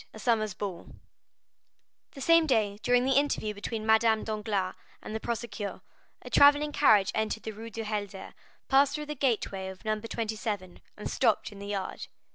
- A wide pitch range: No, average, 3.2 semitones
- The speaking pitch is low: No, high, 220 Hz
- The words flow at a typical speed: Yes, average, 170 wpm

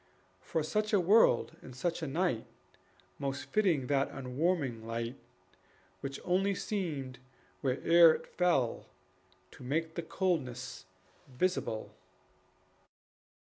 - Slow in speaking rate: Yes, slow, 105 wpm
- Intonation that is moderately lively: No, wide, 5.8 semitones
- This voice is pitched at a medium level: Yes, medium, 150 Hz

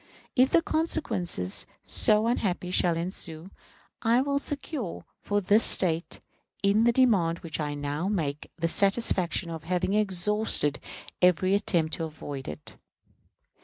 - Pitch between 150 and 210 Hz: Yes, medium, 185 Hz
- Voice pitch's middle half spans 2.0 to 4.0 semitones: No, average, 4.6 semitones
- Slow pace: Yes, slow, 130 wpm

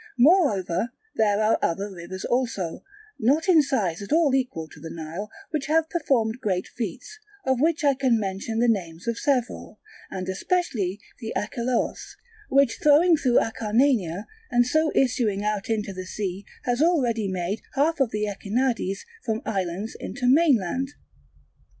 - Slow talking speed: No, average, 150 wpm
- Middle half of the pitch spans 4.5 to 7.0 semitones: Yes, wide, 5.6 semitones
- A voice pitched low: No, high, 225 Hz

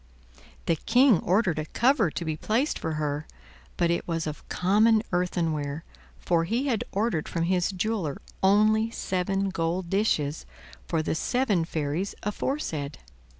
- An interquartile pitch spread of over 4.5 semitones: Yes, average, 5.1 semitones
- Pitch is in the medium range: Yes, medium, 180 Hz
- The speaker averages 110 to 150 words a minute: Yes, average, 145 wpm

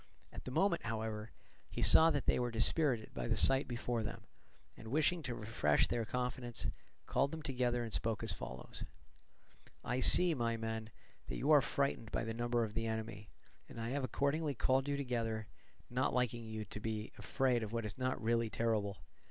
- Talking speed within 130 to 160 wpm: No, average, 190 wpm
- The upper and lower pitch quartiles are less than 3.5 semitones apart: Yes, average, 2.8 semitones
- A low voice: Yes, low, 120 Hz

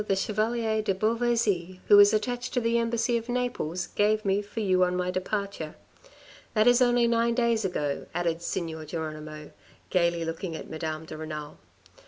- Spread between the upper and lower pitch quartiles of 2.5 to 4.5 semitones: No, wide, 5.6 semitones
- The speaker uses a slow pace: No, average, 170 wpm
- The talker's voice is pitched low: No, high, 200 Hz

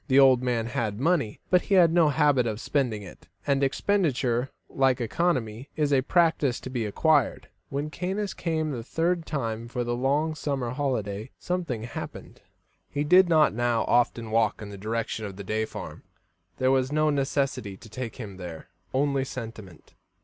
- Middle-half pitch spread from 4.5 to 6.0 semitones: Yes, average, 4.8 semitones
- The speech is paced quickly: No, average, 175 wpm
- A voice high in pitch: No, low, 130 Hz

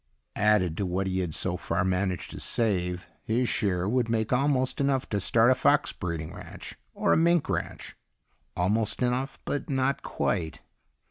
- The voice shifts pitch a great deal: Yes, wide, 5.9 semitones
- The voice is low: Yes, low, 105 Hz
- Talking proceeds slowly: No, average, 170 wpm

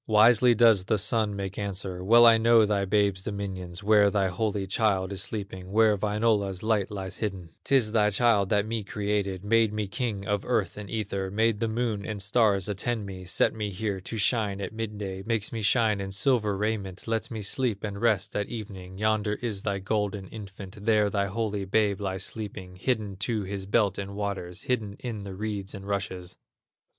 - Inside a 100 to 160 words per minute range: No, average, 190 wpm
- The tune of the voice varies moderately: No, narrow, 2.1 semitones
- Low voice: Yes, low, 105 Hz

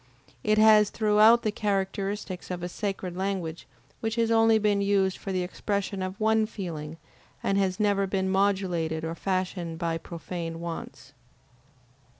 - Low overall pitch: No, high, 195 Hz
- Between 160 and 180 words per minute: No, average, 150 wpm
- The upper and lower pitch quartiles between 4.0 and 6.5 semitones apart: No, average, 2.9 semitones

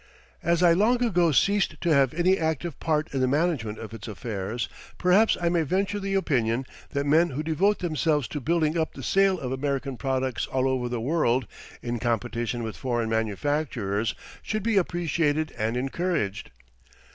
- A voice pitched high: No, medium, 145 Hz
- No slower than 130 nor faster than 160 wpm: No, average, 170 wpm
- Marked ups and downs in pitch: Yes, wide, 6.2 semitones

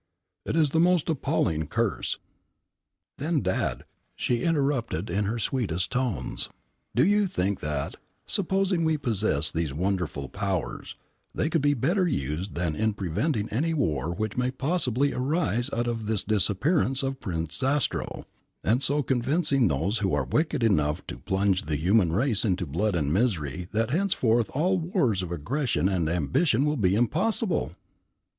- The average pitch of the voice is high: No, low, 115 Hz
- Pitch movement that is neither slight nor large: No, wide, 8.3 semitones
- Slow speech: No, average, 155 wpm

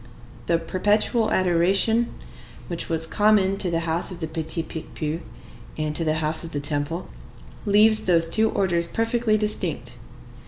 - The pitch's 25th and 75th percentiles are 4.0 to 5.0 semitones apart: Yes, average, 4.5 semitones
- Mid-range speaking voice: Yes, medium, 170 Hz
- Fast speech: No, average, 150 wpm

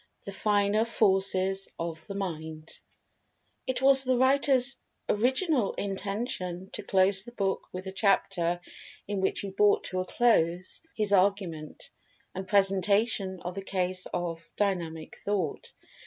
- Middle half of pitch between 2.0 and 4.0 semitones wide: Yes, narrow, 2.4 semitones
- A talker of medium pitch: No, high, 195 Hz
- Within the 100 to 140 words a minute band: Yes, slow, 135 wpm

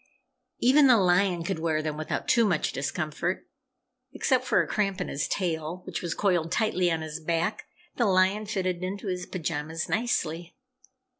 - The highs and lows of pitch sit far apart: No, average, 3.7 semitones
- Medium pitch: Yes, medium, 180 Hz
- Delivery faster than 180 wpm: No, average, 165 wpm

